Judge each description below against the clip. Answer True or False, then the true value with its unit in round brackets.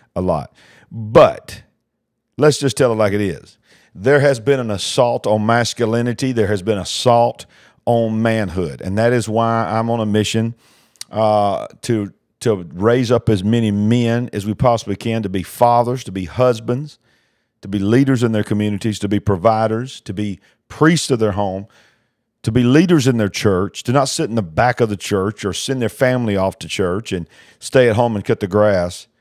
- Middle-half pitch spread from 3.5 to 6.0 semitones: False (2.7 semitones)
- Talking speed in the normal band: True (195 wpm)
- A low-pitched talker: True (115 Hz)